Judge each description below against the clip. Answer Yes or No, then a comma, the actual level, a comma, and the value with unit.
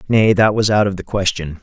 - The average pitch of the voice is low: Yes, low, 100 Hz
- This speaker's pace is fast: Yes, fast, 260 wpm